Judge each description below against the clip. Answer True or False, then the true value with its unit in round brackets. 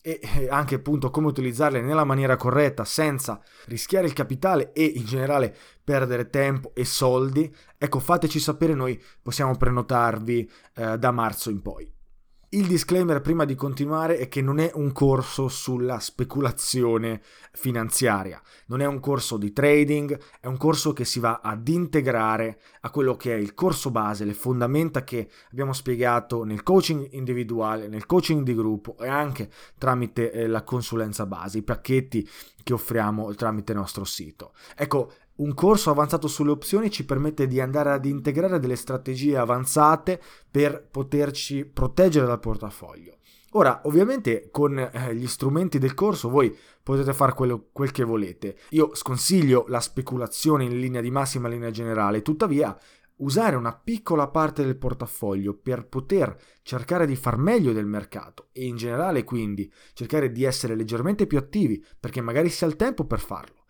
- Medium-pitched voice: False (130 Hz)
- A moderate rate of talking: True (160 wpm)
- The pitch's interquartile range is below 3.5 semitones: False (4.0 semitones)